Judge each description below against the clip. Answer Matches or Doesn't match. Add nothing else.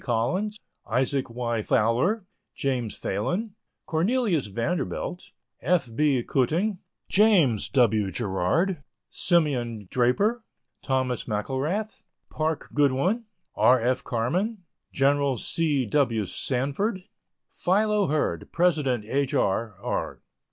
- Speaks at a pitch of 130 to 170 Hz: Matches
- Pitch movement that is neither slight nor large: Doesn't match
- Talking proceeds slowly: Matches